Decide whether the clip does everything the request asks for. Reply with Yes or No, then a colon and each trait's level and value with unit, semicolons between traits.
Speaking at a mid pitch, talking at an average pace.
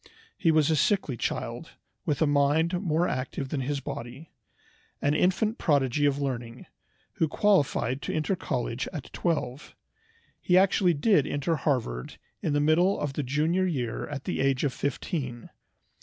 Yes: medium, 145 Hz; average, 155 wpm